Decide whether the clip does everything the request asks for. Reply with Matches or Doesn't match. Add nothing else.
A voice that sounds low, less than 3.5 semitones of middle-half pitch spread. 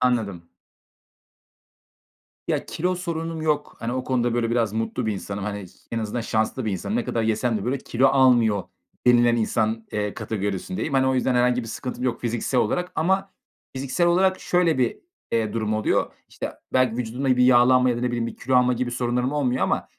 Matches